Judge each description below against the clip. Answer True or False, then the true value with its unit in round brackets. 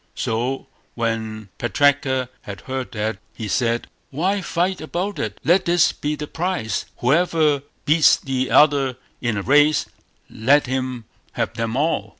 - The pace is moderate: True (145 wpm)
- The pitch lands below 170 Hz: True (135 Hz)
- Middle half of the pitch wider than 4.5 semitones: True (5.0 semitones)